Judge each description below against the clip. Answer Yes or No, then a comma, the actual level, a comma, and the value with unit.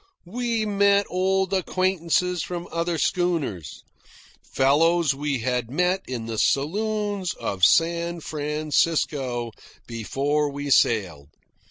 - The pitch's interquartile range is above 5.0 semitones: Yes, wide, 5.4 semitones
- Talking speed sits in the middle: No, slow, 100 wpm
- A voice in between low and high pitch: Yes, medium, 165 Hz